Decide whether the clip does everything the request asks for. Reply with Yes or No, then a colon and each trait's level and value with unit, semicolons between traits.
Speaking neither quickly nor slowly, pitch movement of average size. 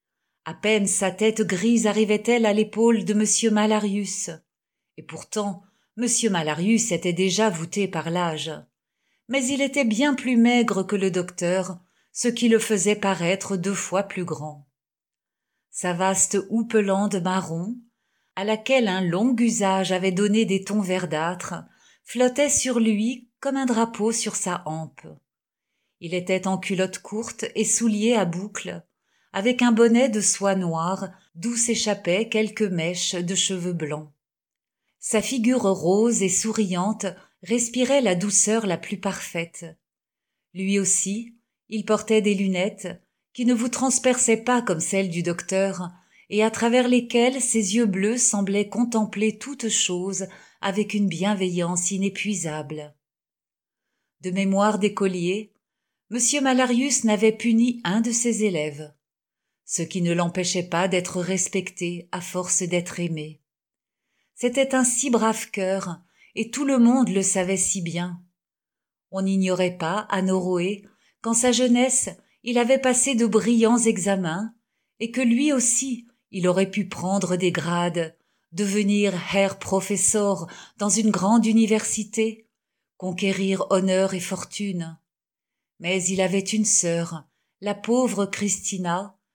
No: slow, 135 wpm; average, 3.5 semitones